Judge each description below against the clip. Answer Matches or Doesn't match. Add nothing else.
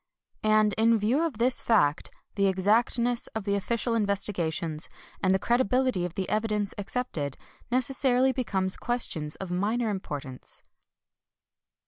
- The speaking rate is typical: Doesn't match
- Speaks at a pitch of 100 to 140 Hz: Doesn't match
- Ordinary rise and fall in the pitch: Matches